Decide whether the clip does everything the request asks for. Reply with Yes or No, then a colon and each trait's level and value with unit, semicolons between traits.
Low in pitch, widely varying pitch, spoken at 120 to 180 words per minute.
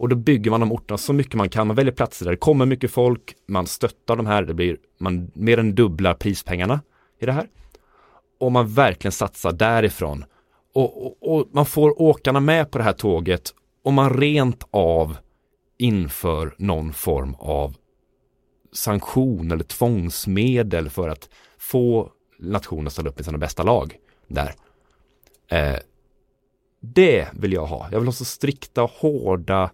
Yes: low, 105 Hz; wide, 6.7 semitones; average, 165 wpm